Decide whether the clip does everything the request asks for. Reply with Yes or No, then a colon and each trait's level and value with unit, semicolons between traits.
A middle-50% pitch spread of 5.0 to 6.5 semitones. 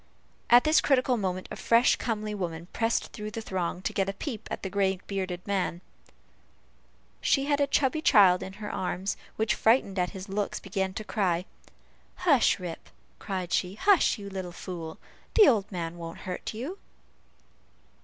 No: average, 4.0 semitones